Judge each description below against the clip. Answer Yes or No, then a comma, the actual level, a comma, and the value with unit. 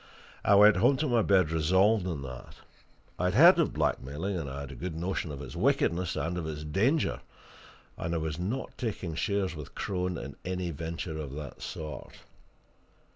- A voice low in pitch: Yes, very low, 85 Hz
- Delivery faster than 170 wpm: Yes, average, 180 wpm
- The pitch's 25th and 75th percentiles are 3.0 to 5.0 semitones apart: Yes, average, 4.5 semitones